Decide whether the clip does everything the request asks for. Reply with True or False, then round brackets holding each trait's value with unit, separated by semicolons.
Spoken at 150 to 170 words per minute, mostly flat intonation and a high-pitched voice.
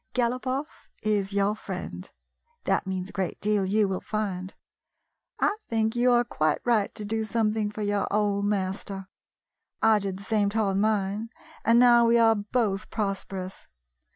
True (155 wpm; 2.2 semitones; 210 Hz)